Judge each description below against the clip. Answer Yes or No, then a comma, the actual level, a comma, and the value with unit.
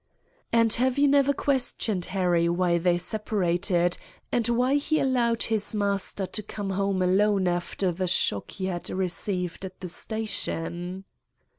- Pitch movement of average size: Yes, average, 4.0 semitones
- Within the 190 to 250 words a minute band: No, average, 145 wpm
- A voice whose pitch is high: Yes, high, 195 Hz